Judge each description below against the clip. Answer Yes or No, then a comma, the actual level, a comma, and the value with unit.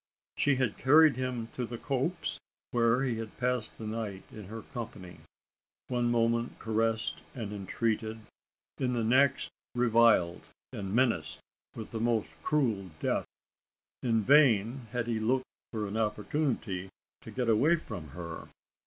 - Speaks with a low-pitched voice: Yes, low, 115 Hz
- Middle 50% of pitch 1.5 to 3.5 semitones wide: Yes, average, 2.8 semitones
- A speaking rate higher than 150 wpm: No, average, 145 wpm